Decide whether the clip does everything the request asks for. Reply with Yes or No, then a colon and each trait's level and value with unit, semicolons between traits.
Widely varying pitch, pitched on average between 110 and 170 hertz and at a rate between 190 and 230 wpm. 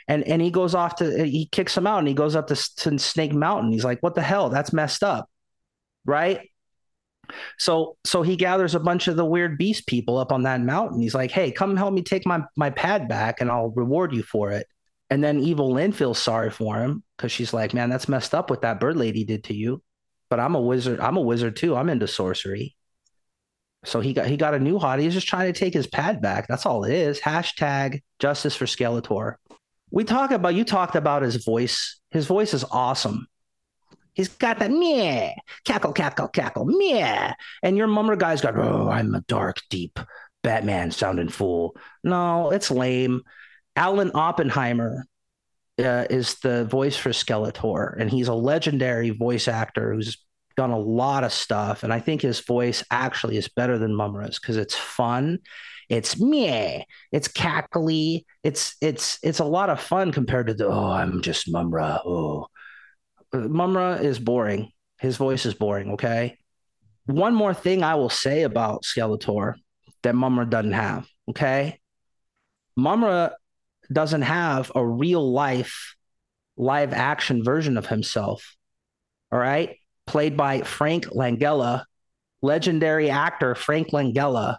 No: wide, 6.0 semitones; low, 135 Hz; average, 175 wpm